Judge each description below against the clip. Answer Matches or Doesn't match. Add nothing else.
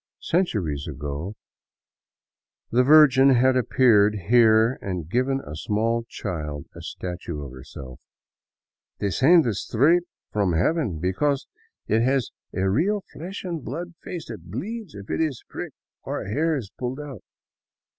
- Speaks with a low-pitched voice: Matches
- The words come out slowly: Doesn't match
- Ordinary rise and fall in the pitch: Doesn't match